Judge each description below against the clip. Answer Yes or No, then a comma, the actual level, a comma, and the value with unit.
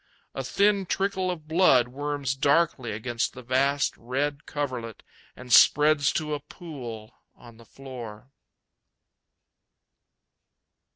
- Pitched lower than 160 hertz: Yes, low, 135 Hz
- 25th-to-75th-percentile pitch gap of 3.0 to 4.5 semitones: Yes, average, 3.8 semitones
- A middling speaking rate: No, slow, 110 wpm